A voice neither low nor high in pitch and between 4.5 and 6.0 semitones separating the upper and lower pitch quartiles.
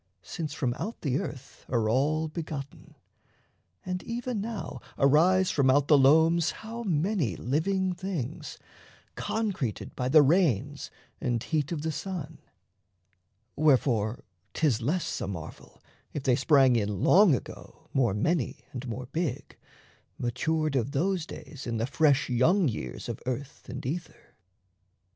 Yes: medium, 145 Hz; average, 5.1 semitones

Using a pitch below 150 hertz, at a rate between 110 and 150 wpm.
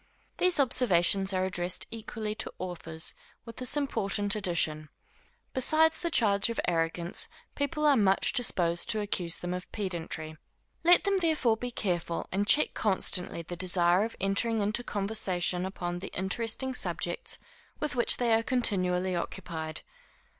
No: high, 200 Hz; average, 145 wpm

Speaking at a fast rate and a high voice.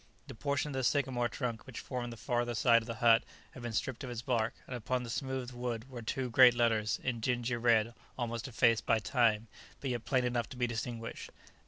No: fast, 220 wpm; low, 120 Hz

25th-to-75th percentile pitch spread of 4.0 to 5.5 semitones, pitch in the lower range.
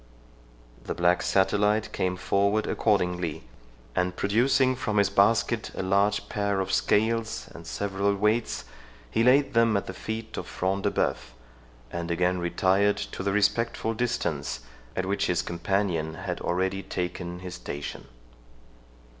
No: average, 2.8 semitones; low, 100 Hz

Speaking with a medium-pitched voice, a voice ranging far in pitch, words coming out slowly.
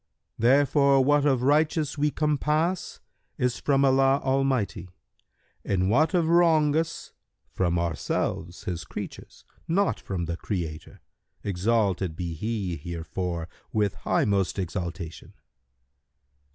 No: low, 115 Hz; wide, 8.6 semitones; slow, 105 wpm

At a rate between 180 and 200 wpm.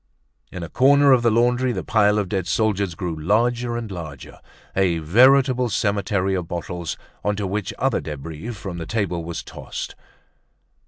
No: average, 160 wpm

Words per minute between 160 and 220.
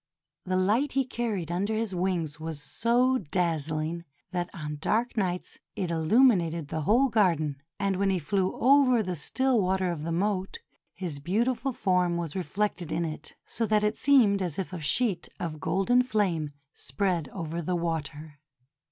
Yes: average, 165 wpm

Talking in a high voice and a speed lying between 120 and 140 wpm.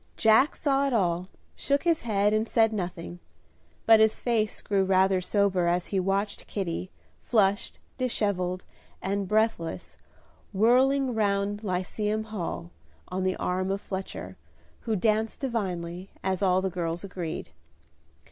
Yes: high, 200 Hz; slow, 135 wpm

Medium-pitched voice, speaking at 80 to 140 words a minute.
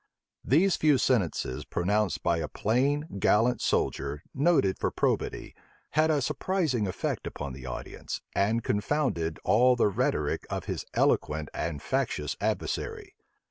No: low, 105 Hz; slow, 135 wpm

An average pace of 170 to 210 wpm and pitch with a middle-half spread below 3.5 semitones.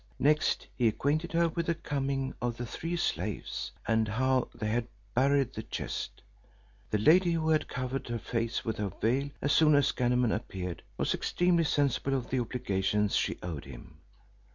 No: average, 175 wpm; average, 4.8 semitones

